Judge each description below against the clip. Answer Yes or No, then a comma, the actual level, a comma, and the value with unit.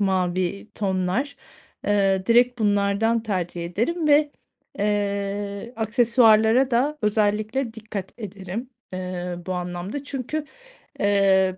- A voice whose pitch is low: No, high, 205 Hz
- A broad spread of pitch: No, average, 3.6 semitones